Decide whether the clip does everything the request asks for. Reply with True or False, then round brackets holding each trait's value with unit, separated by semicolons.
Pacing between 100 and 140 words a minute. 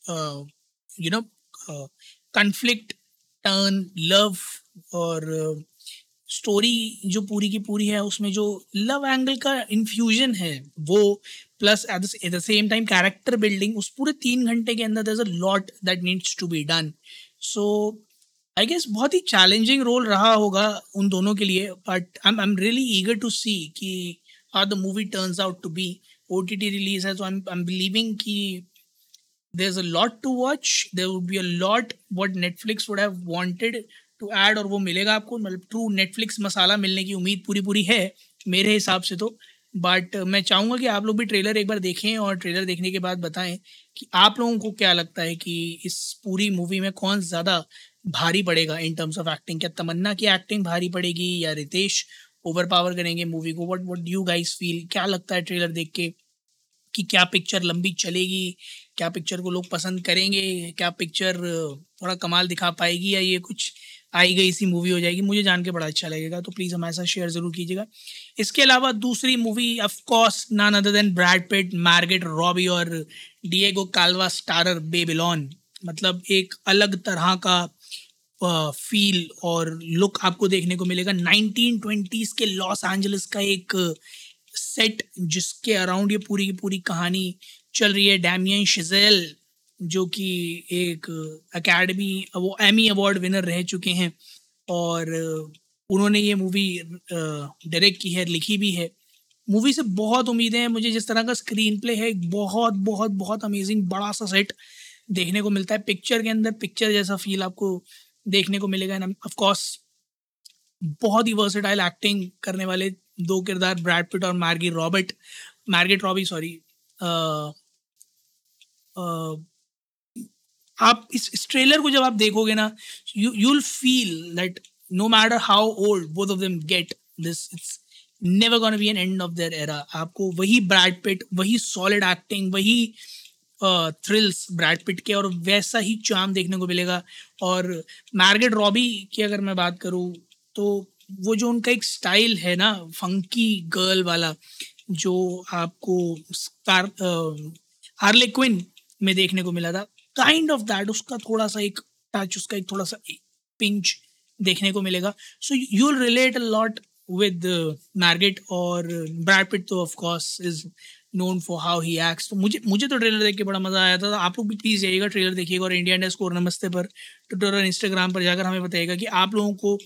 False (170 wpm)